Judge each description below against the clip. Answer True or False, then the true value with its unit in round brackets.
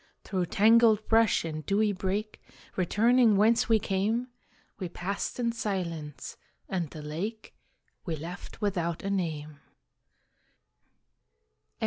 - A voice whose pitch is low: False (195 Hz)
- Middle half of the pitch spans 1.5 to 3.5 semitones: False (4.4 semitones)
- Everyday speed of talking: False (110 wpm)